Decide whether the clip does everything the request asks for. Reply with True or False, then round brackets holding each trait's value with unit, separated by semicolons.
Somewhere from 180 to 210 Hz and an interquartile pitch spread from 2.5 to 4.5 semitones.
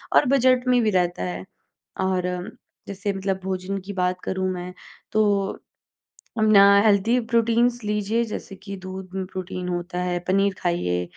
True (190 Hz; 2.9 semitones)